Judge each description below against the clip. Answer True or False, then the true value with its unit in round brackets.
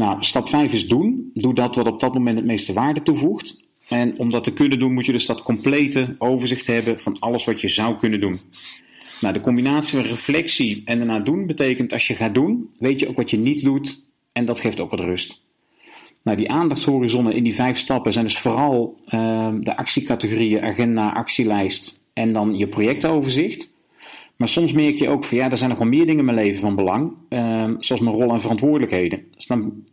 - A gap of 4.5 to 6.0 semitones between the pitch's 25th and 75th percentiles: False (3.2 semitones)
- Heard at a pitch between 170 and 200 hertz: False (120 Hz)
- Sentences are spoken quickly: True (215 wpm)